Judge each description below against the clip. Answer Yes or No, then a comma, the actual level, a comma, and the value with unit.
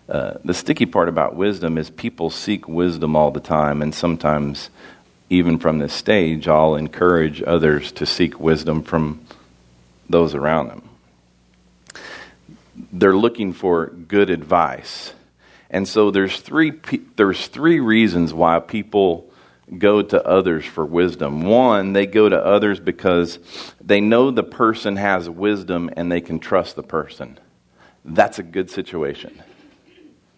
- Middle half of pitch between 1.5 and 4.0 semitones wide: No, average, 4.8 semitones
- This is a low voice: Yes, very low, 85 Hz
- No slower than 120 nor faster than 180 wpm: Yes, average, 140 wpm